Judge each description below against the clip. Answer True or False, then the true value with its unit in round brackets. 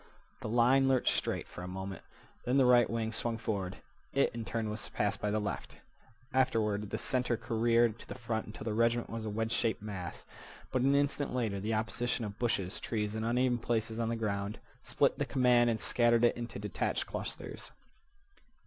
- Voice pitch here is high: False (115 Hz)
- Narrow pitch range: True (2.1 semitones)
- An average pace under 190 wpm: False (195 wpm)